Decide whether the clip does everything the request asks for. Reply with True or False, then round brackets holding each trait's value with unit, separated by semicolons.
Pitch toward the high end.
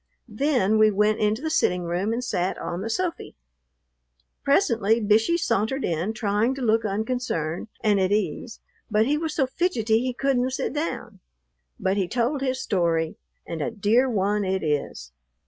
True (220 Hz)